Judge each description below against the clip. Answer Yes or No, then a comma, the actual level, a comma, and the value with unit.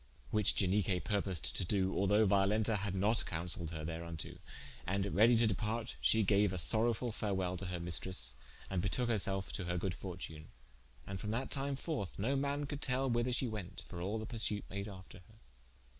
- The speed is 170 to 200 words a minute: Yes, average, 190 wpm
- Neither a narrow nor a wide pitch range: Yes, average, 3.5 semitones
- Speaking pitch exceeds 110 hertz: No, low, 100 Hz